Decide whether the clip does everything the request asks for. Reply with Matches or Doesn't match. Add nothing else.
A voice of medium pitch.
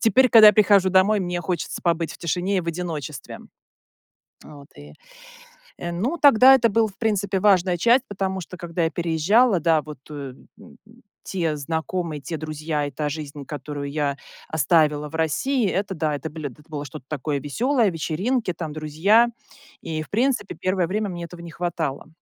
Matches